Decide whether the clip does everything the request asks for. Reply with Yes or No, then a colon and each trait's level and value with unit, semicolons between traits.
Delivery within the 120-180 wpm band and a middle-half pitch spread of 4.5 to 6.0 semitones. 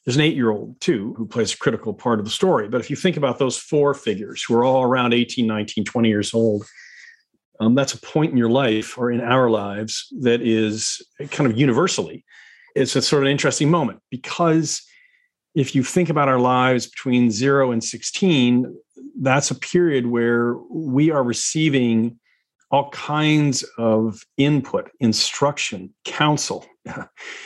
No: average, 165 wpm; average, 3.7 semitones